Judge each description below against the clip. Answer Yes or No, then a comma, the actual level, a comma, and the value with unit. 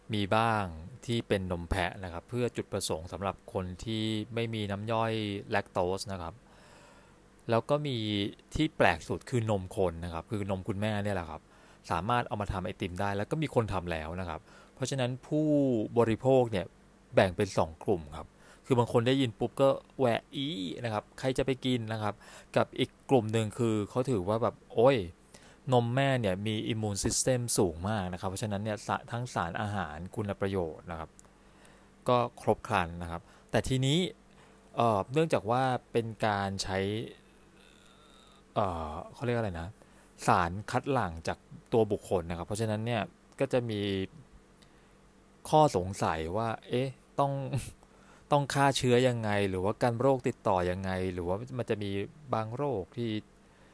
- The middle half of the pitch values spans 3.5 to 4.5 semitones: Yes, average, 4.2 semitones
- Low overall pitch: Yes, low, 110 Hz